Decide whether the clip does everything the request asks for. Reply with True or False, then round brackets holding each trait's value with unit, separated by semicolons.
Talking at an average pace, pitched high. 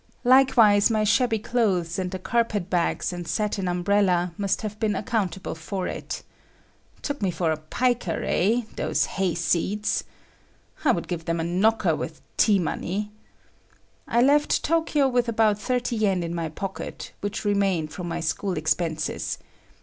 True (150 wpm; 200 Hz)